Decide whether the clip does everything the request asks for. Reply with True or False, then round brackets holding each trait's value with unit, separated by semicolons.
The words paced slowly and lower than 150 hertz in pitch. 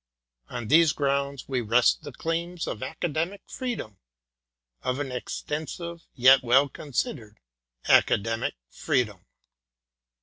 True (105 wpm; 140 Hz)